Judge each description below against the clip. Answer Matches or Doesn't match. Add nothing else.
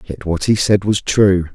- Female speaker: Doesn't match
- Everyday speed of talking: Doesn't match